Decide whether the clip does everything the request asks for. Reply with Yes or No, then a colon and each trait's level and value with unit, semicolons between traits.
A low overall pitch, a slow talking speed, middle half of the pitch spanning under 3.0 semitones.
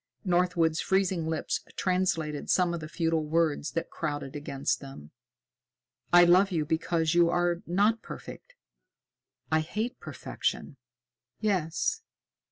No: medium, 170 Hz; slow, 120 wpm; narrow, 2.5 semitones